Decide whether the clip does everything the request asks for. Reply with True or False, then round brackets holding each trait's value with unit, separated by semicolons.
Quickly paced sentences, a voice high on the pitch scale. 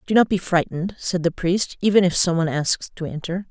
False (240 wpm; 180 Hz)